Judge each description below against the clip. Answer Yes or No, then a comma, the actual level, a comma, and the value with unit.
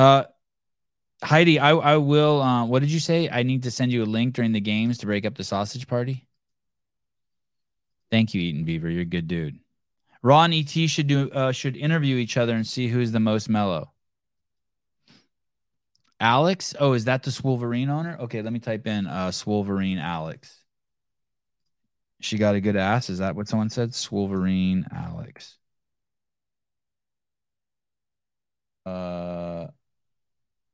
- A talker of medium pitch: No, low, 120 Hz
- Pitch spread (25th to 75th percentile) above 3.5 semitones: Yes, average, 4.8 semitones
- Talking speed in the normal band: Yes, average, 150 wpm